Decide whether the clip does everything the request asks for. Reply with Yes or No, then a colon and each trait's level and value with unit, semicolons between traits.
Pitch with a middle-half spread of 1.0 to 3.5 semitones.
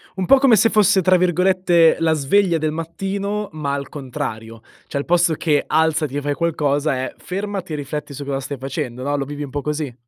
No: average, 4.4 semitones